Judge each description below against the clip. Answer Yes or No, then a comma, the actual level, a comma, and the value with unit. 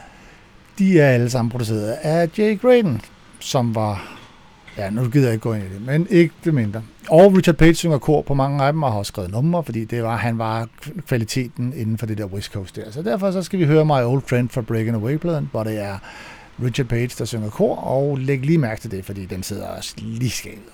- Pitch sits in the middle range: No, low, 125 Hz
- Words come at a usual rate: No, fast, 235 wpm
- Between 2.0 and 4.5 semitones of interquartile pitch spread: No, wide, 5.6 semitones